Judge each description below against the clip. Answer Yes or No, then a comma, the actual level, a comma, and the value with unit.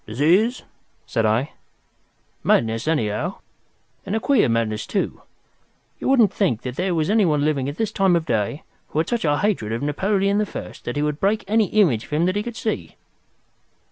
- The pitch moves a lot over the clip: Yes, wide, 8.4 semitones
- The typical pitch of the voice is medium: Yes, medium, 165 Hz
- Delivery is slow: No, average, 185 wpm